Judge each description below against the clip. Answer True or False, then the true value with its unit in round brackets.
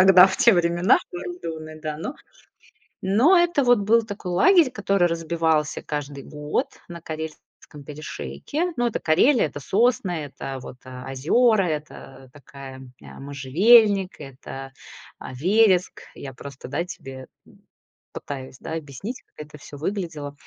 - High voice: False (165 Hz)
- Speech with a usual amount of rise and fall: False (6.3 semitones)